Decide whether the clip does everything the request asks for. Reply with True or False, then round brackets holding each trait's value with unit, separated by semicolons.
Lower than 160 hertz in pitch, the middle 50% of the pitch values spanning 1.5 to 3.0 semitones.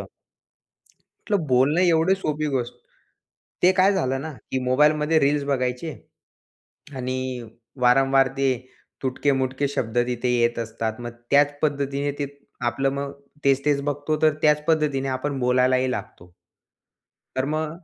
True (140 Hz; 2.7 semitones)